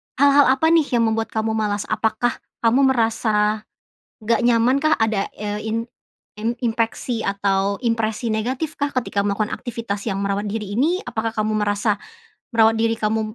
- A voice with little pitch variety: Yes, narrow, 2.2 semitones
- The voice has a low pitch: No, high, 225 Hz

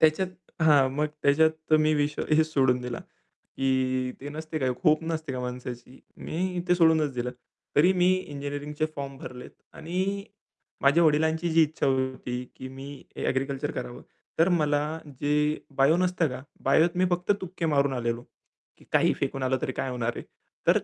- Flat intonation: No, average, 3.4 semitones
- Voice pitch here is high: No, medium, 145 Hz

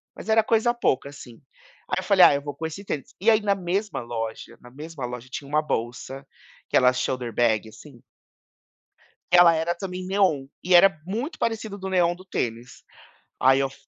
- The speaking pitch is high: No, medium, 160 Hz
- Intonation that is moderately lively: No, wide, 7.1 semitones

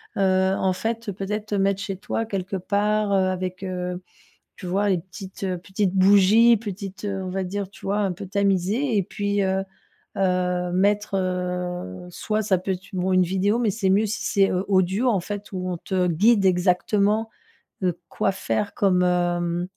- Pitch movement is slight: Yes, narrow, 1.9 semitones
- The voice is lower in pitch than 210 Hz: Yes, high, 190 Hz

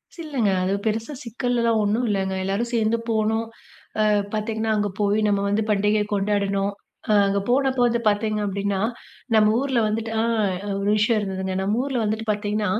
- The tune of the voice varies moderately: No, narrow, 2.1 semitones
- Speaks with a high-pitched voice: Yes, high, 215 Hz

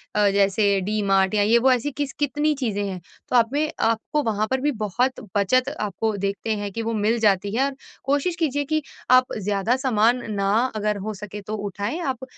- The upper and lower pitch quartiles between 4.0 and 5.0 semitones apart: Yes, average, 4.4 semitones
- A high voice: Yes, high, 225 Hz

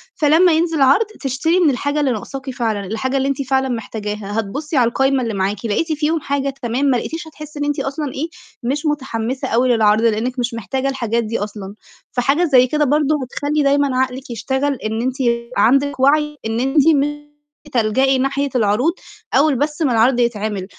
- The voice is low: No, very high, 265 Hz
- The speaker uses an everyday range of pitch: Yes, average, 4.0 semitones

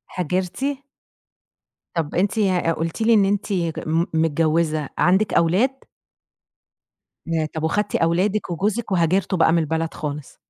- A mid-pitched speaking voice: Yes, medium, 170 Hz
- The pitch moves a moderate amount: Yes, average, 3.4 semitones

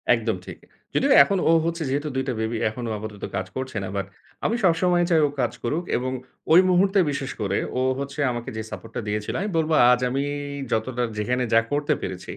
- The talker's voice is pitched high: No, low, 130 Hz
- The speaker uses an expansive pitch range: Yes, wide, 6.2 semitones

